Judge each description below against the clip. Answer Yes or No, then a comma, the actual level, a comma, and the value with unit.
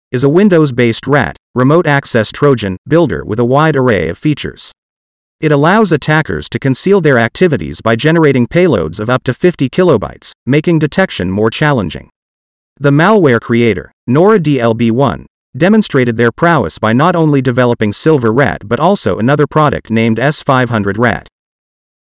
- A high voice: No, low, 135 Hz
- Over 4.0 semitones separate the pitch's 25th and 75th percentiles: Yes, average, 5.2 semitones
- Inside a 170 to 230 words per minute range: No, average, 150 wpm